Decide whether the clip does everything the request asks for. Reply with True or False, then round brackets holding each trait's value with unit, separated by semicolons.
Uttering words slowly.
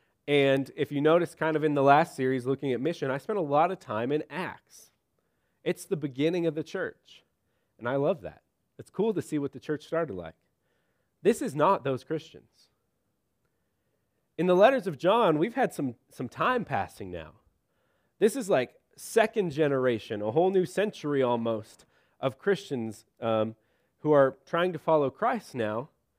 False (175 wpm)